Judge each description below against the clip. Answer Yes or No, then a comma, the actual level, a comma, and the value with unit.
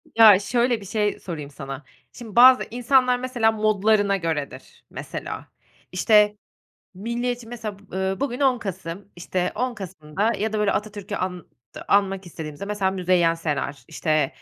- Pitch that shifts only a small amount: No, average, 4.3 semitones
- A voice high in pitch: Yes, high, 205 Hz